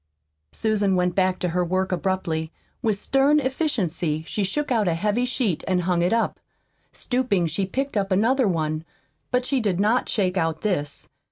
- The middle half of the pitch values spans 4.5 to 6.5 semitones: Yes, average, 5.2 semitones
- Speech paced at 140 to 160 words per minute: No, average, 175 wpm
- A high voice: Yes, high, 195 Hz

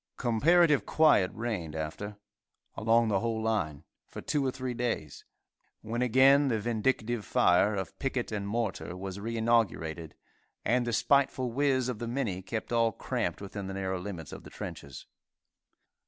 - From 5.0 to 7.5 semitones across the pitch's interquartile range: No, average, 4.2 semitones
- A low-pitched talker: Yes, low, 115 Hz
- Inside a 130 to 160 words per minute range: Yes, average, 155 wpm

